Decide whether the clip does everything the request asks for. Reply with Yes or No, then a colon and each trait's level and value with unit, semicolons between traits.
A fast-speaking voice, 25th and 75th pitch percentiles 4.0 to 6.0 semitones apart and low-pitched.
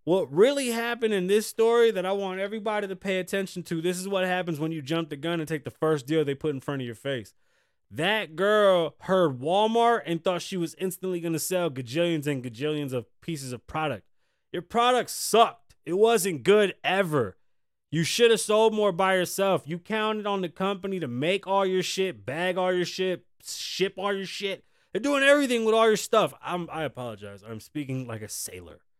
No: fast, 210 wpm; average, 4.4 semitones; medium, 185 Hz